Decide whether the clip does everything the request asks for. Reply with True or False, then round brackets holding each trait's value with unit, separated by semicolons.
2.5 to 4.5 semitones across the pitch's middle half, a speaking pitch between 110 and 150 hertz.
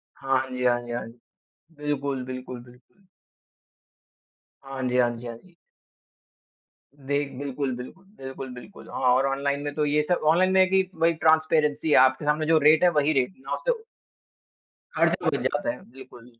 True (3.5 semitones; 140 Hz)